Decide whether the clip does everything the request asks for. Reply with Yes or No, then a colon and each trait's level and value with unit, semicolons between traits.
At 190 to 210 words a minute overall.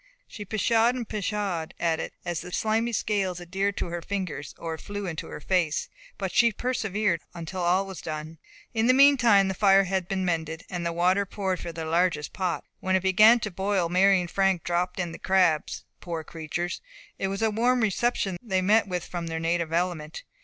Yes: average, 195 wpm